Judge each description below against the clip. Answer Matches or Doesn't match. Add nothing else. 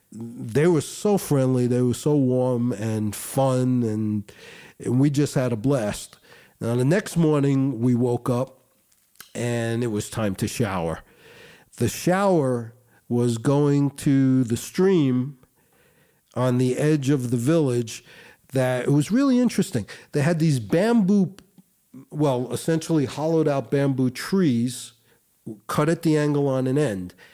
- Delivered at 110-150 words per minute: Matches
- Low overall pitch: Matches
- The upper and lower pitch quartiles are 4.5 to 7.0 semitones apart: Doesn't match